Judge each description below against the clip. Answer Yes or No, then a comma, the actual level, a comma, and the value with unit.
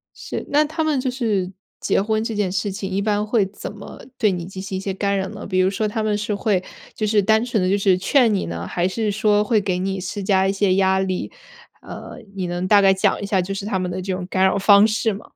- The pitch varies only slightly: Yes, narrow, 2.2 semitones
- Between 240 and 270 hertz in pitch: No, high, 200 Hz